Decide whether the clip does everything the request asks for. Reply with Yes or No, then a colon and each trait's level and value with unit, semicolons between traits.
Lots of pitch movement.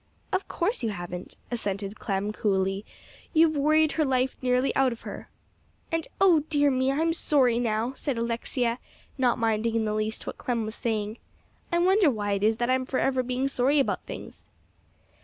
No: average, 4.7 semitones